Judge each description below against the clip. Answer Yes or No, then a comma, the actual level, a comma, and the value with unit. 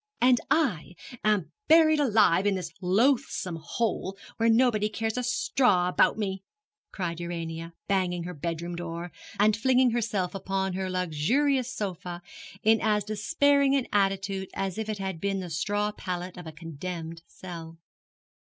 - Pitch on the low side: No, high, 195 Hz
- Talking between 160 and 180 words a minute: No, average, 150 wpm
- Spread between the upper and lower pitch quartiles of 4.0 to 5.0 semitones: Yes, average, 4.3 semitones